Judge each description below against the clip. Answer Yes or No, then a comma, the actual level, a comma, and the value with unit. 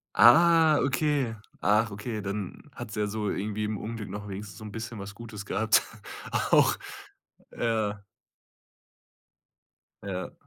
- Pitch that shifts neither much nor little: No, narrow, 2.3 semitones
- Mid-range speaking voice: No, low, 110 Hz